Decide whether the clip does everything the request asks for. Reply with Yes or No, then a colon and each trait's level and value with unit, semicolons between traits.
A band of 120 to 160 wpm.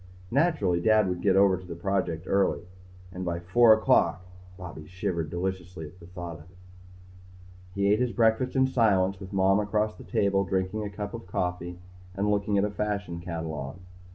No: average, 180 wpm